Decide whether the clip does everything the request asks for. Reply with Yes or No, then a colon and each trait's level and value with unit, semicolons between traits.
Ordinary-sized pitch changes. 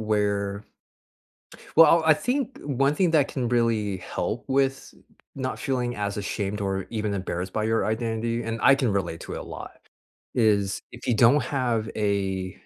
Yes: average, 4.6 semitones